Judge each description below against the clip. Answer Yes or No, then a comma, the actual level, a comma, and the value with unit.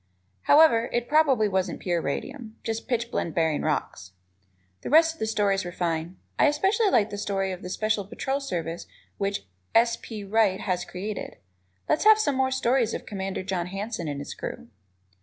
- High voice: Yes, high, 210 Hz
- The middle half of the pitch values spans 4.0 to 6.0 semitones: Yes, average, 5.2 semitones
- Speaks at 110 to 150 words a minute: No, average, 175 wpm